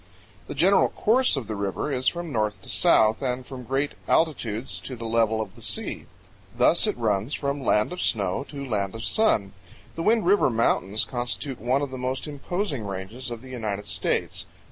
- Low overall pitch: Yes, low, 125 Hz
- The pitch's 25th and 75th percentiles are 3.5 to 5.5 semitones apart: Yes, average, 4.8 semitones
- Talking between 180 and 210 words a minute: Yes, average, 190 wpm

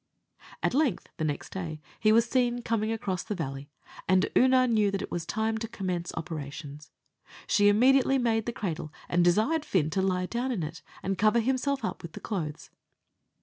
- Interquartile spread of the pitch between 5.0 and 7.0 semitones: Yes, wide, 5.6 semitones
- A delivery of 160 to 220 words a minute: Yes, average, 190 wpm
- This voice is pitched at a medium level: No, high, 205 Hz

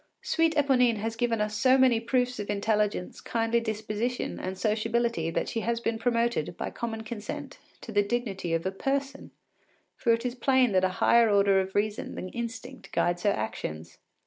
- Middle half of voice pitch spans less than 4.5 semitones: Yes, average, 2.9 semitones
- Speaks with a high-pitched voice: Yes, high, 225 Hz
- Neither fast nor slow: Yes, average, 180 wpm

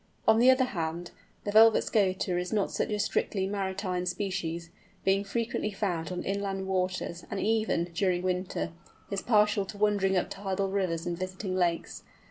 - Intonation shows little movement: Yes, narrow, 2.1 semitones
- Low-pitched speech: No, high, 190 Hz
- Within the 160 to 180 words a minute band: Yes, average, 165 wpm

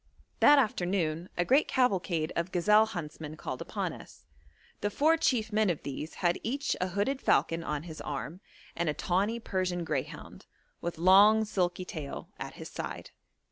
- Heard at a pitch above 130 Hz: Yes, medium, 185 Hz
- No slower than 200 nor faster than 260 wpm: No, average, 165 wpm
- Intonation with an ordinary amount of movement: Yes, average, 4.6 semitones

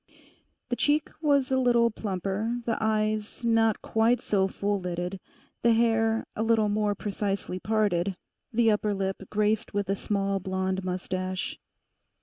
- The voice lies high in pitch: Yes, high, 210 Hz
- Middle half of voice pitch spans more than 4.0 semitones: No, average, 2.7 semitones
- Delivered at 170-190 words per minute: No, average, 140 wpm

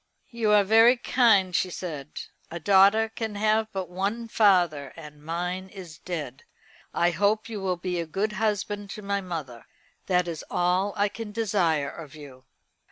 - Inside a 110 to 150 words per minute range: No, average, 165 wpm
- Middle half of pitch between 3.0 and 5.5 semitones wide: Yes, average, 3.8 semitones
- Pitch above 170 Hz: Yes, high, 190 Hz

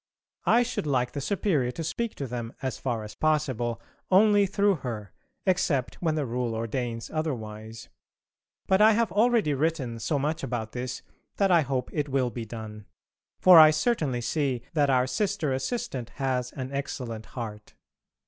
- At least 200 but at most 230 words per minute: No, average, 165 wpm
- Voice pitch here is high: No, low, 135 Hz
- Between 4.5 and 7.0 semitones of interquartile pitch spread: Yes, wide, 5.5 semitones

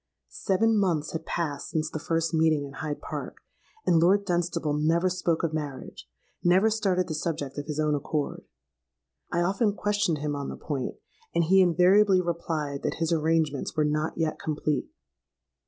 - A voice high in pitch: No, medium, 165 Hz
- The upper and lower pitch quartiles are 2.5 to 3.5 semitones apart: Yes, average, 2.9 semitones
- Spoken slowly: No, average, 165 wpm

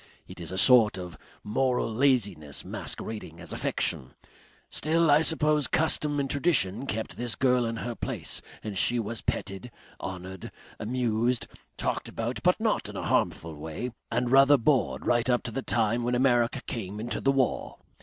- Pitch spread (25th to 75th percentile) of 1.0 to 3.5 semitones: No, average, 4.2 semitones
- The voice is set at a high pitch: No, low, 120 Hz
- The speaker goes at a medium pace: Yes, average, 165 wpm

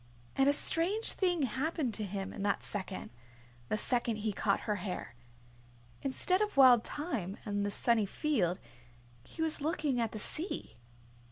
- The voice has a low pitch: No, high, 235 Hz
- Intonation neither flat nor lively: No, wide, 7.0 semitones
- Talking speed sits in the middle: Yes, average, 160 wpm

